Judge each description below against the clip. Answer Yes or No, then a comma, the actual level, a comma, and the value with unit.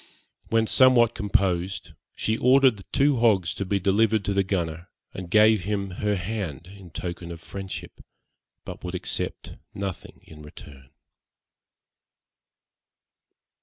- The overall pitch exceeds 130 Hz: No, low, 100 Hz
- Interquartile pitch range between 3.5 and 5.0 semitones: Yes, average, 3.9 semitones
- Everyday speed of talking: No, slow, 130 wpm